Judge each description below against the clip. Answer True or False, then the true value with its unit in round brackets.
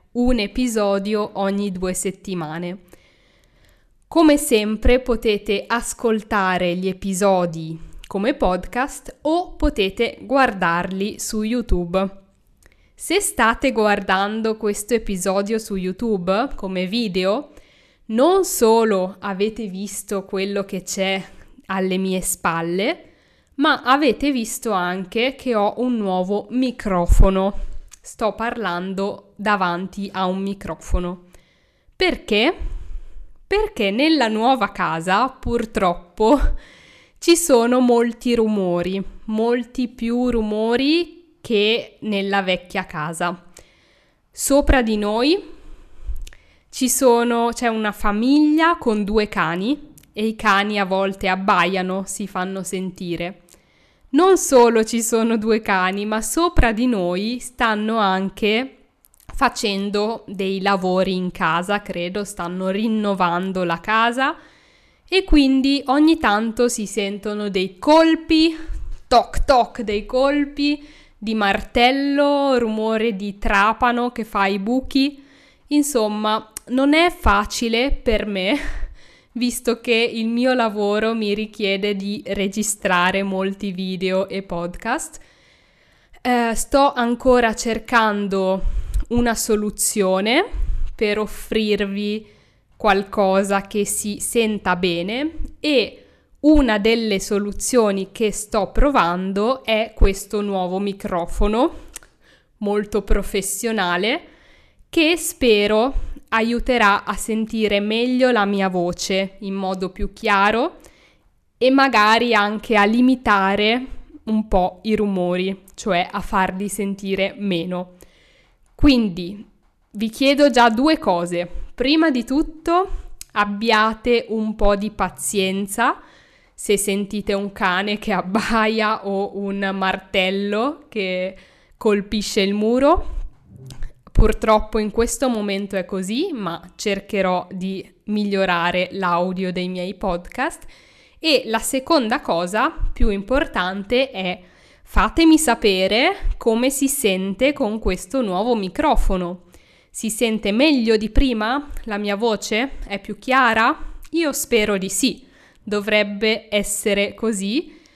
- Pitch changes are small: False (3.9 semitones)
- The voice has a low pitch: False (215 Hz)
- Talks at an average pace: False (105 wpm)